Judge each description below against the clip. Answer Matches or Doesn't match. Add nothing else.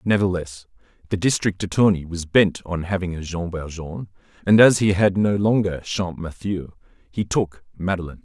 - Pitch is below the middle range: Matches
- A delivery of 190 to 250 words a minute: Doesn't match